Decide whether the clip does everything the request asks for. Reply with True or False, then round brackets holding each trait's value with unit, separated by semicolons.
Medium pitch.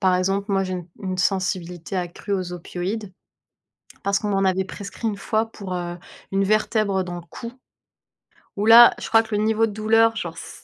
False (195 Hz)